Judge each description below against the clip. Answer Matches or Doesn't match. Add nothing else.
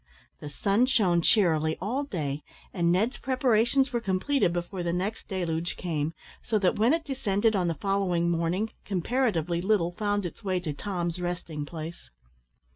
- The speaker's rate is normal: Matches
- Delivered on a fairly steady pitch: Doesn't match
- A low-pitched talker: Doesn't match